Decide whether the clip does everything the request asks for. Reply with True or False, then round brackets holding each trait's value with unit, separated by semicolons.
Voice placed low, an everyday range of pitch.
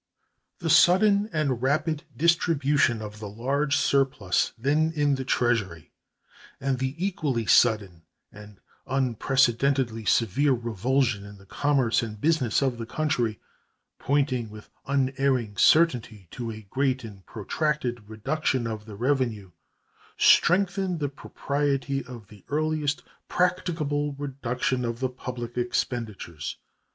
True (130 Hz; 4.4 semitones)